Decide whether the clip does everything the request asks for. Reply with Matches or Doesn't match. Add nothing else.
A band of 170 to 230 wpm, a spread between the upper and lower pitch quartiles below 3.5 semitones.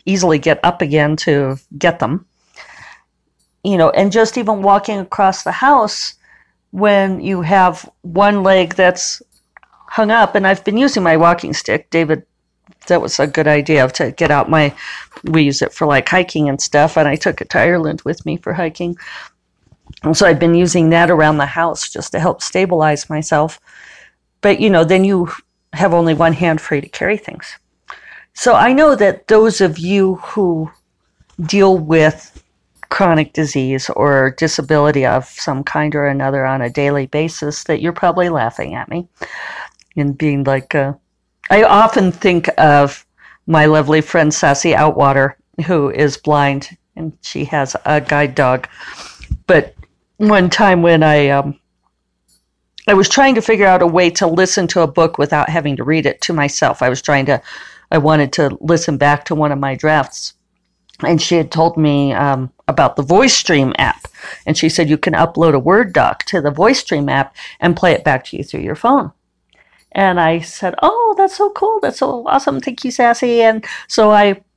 Doesn't match